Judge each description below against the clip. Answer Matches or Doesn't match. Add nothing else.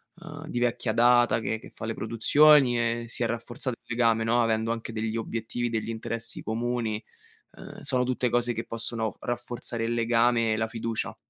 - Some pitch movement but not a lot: Doesn't match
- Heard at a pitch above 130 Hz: Doesn't match